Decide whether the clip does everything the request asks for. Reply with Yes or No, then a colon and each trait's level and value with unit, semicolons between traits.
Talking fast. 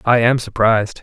No: average, 175 wpm